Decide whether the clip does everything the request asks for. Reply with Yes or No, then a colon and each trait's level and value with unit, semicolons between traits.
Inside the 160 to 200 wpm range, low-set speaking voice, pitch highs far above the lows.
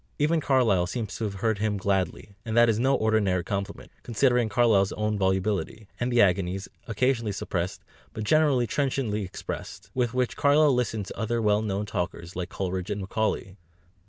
No: average, 170 wpm; low, 105 Hz; average, 3.7 semitones